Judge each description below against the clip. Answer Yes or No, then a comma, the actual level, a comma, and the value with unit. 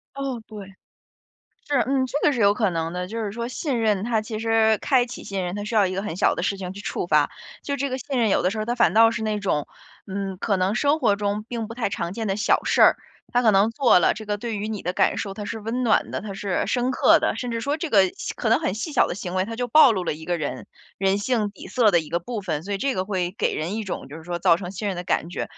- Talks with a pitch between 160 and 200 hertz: No, high, 210 Hz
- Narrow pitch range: No, average, 3.7 semitones